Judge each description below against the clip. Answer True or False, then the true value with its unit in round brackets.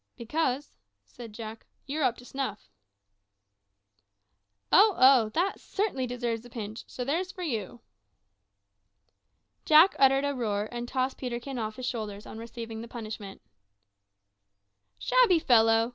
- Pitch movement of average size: True (3.6 semitones)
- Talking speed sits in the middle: False (130 wpm)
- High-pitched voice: True (245 Hz)